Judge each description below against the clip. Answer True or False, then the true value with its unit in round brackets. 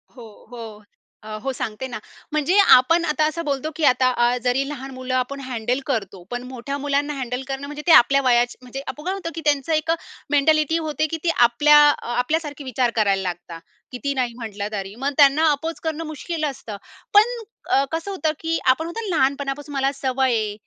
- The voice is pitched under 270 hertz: False (275 Hz)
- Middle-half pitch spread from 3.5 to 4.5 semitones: True (3.8 semitones)